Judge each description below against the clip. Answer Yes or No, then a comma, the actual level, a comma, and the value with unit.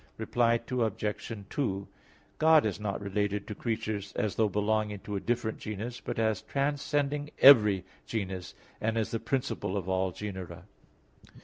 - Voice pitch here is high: No, low, 110 Hz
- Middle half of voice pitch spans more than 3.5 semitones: No, average, 3.1 semitones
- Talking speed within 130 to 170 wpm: Yes, average, 145 wpm